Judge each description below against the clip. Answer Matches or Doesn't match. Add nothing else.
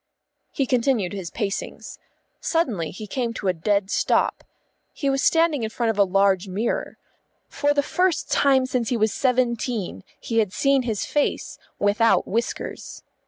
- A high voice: Matches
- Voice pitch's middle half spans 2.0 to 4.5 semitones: Doesn't match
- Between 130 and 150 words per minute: Doesn't match